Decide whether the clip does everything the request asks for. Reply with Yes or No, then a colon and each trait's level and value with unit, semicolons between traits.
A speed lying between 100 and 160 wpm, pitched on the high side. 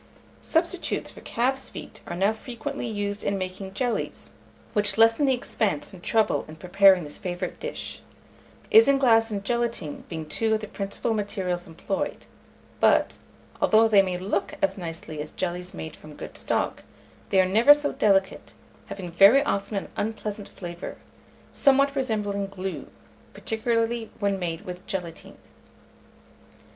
Yes: average, 145 wpm; high, 200 Hz